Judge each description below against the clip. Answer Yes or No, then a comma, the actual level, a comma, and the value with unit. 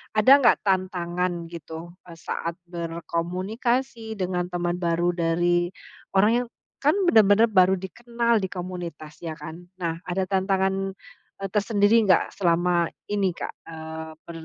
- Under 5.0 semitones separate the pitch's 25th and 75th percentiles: Yes, average, 2.9 semitones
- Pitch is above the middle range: No, medium, 180 Hz